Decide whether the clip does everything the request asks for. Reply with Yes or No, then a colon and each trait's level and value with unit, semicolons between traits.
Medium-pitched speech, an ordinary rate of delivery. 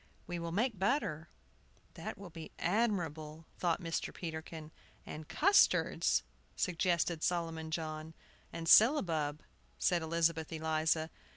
No: medium, 165 Hz; slow, 110 wpm